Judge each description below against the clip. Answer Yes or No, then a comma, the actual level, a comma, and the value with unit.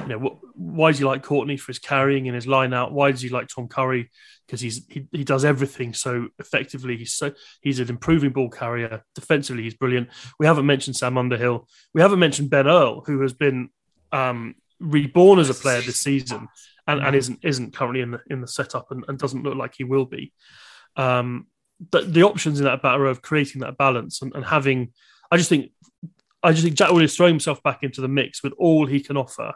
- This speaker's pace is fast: Yes, fast, 220 wpm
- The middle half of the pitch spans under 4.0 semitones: Yes, average, 2.8 semitones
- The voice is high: No, low, 135 Hz